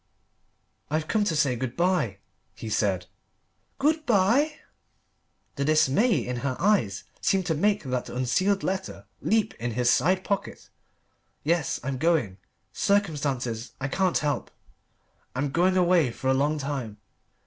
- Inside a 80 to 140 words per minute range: Yes, slow, 135 wpm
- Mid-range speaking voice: Yes, medium, 150 Hz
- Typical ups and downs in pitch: No, wide, 6.9 semitones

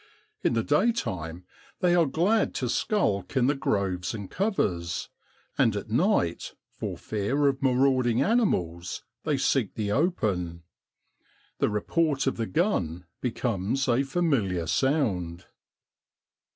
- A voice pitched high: No, low, 120 Hz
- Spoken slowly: Yes, slow, 125 wpm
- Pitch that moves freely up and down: Yes, wide, 8.0 semitones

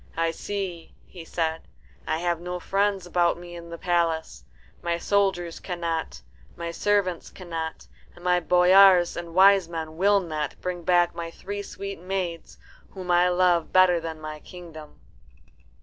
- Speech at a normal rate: Yes, average, 150 wpm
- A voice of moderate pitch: Yes, medium, 175 Hz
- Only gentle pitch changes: Yes, narrow, 1.7 semitones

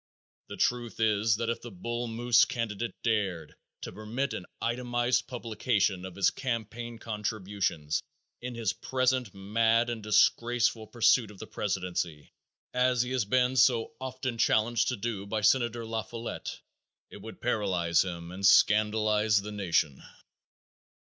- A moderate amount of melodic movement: Yes, average, 3.0 semitones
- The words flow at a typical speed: Yes, average, 145 wpm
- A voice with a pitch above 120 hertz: No, low, 115 Hz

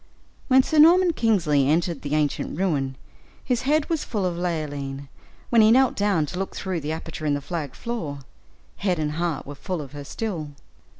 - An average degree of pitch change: No, wide, 7.1 semitones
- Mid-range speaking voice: Yes, medium, 170 Hz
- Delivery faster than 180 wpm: Yes, average, 190 wpm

